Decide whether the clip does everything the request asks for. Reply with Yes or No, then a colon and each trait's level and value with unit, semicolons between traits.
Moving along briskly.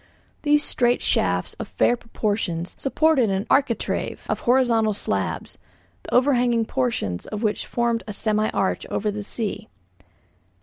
No: slow, 135 wpm